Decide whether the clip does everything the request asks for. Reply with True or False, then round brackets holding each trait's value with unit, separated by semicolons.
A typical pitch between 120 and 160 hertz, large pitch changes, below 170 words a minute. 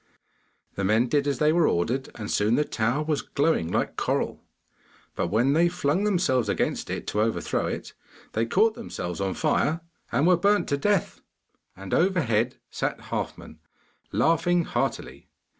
True (140 Hz; 7.6 semitones; 160 wpm)